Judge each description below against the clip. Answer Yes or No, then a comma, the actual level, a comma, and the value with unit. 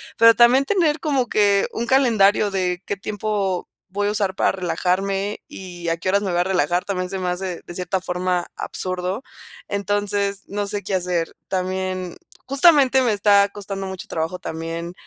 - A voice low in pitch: No, high, 195 Hz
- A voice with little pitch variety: Yes, narrow, 2.2 semitones